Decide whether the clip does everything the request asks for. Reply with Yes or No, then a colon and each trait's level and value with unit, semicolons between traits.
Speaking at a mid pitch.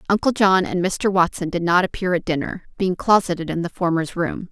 Yes: medium, 180 Hz